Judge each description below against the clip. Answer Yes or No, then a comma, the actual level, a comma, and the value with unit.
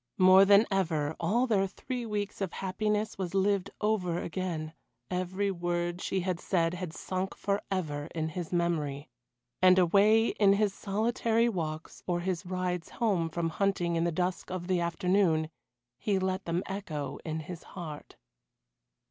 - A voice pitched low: No, medium, 185 Hz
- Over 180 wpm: No, average, 155 wpm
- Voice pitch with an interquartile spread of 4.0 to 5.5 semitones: No, average, 2.8 semitones